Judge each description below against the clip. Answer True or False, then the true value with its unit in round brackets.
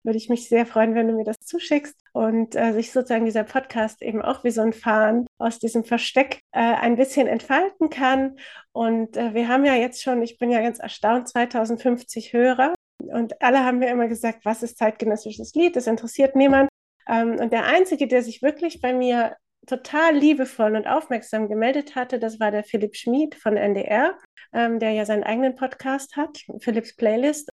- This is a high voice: True (235 Hz)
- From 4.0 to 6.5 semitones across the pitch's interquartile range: False (2.8 semitones)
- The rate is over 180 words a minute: True (190 wpm)